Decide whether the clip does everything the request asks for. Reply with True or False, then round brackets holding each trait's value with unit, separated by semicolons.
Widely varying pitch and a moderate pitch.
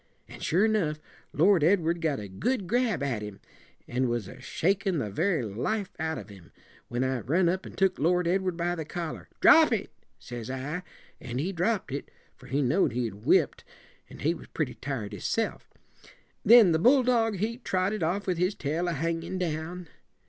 True (6.2 semitones; 165 Hz)